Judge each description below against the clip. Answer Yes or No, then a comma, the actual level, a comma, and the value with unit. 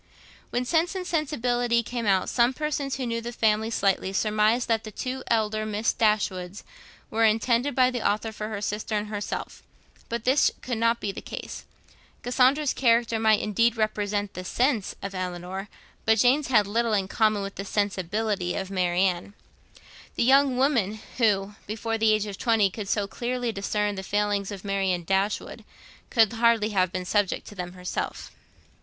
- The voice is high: Yes, high, 215 Hz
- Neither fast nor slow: Yes, average, 175 wpm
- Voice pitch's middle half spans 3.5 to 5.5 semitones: No, average, 3.1 semitones